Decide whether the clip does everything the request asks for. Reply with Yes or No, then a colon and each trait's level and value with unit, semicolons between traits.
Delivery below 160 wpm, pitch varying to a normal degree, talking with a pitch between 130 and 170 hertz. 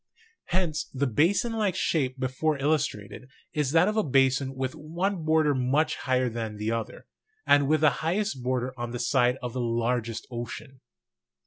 No: average, 170 wpm; average, 4.1 semitones; low, 135 Hz